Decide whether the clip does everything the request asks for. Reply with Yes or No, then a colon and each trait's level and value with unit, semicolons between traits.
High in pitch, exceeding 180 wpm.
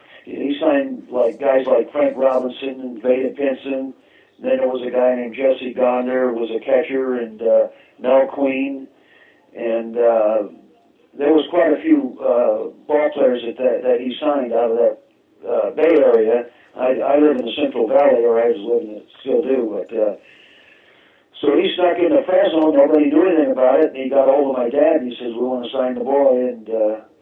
No: low, 135 Hz; fast, 205 wpm